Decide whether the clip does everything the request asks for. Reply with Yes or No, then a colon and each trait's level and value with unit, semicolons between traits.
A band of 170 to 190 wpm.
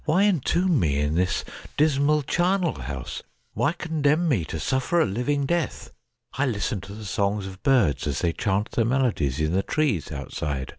Yes: average, 185 wpm